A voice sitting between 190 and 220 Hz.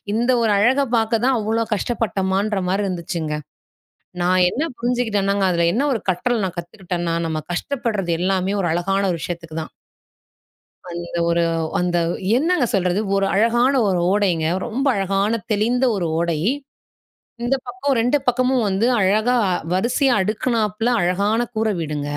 Yes: high, 205 Hz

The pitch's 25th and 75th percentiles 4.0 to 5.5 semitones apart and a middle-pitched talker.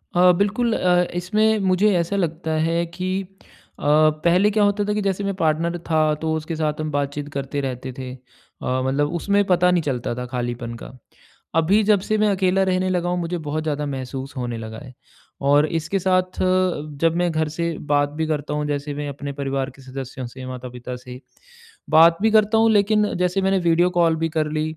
Yes: average, 4.5 semitones; medium, 160 Hz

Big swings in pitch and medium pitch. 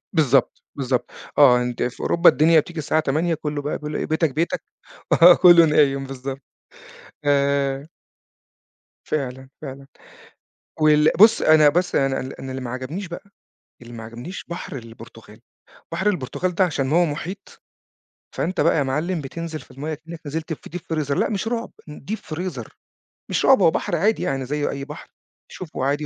No: average, 3.7 semitones; medium, 150 Hz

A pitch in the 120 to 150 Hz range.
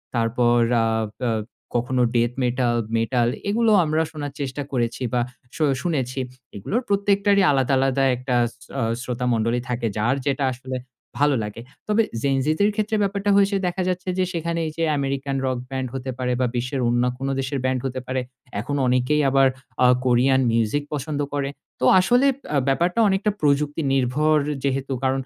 Yes: low, 135 Hz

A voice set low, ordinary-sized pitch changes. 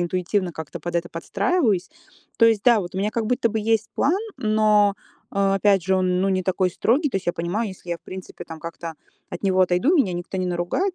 No: high, 195 Hz; average, 3.6 semitones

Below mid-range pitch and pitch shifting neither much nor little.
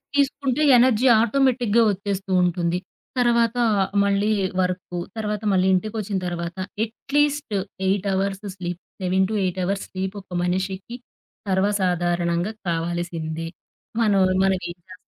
No: high, 195 Hz; average, 3.4 semitones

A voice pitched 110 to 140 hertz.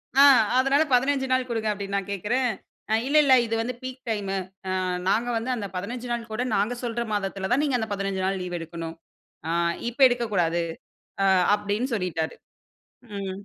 No: high, 220 Hz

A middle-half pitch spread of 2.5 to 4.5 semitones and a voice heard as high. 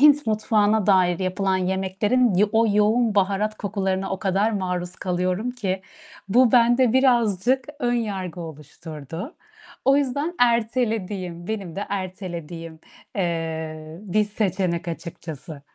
Yes: average, 3.9 semitones; high, 195 Hz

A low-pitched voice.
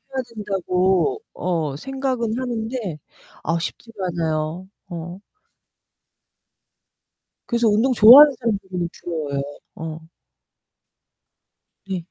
No: high, 190 Hz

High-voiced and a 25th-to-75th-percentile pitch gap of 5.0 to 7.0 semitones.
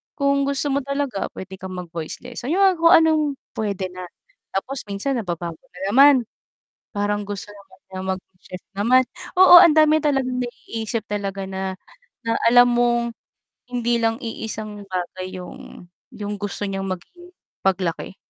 Yes: high, 215 Hz; wide, 5.6 semitones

